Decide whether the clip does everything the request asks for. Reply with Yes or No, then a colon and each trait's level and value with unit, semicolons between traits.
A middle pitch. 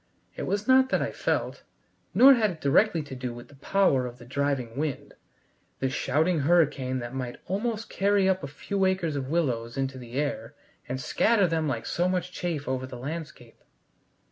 Yes: medium, 145 Hz